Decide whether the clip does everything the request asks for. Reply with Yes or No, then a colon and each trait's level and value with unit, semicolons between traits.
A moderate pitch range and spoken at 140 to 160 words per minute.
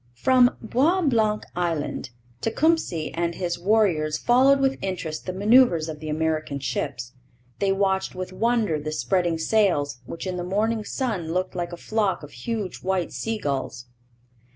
No: wide, 5.8 semitones; average, 155 wpm